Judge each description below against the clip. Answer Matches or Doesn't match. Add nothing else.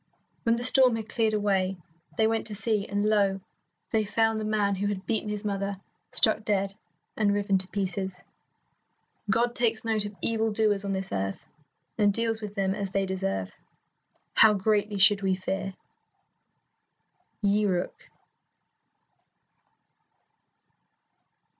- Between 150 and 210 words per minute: Doesn't match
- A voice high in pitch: Matches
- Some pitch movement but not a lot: Doesn't match